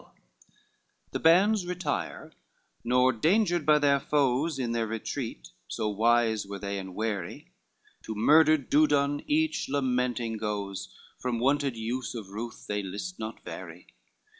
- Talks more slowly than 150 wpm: Yes, average, 140 wpm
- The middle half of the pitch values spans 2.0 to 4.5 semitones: No, average, 5.1 semitones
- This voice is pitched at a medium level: No, low, 125 Hz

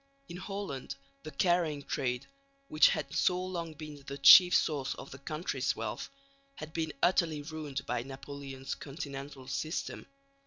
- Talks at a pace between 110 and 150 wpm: Yes, average, 145 wpm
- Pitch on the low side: No, medium, 145 Hz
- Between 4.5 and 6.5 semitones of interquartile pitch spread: No, average, 3.0 semitones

